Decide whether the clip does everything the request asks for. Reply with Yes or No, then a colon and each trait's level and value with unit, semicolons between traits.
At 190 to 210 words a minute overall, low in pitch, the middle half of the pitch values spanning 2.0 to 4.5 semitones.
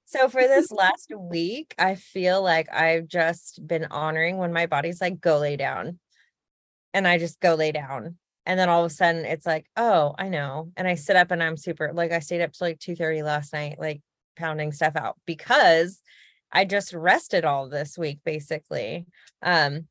No: average, 200 wpm; medium, 165 Hz; narrow, 2.5 semitones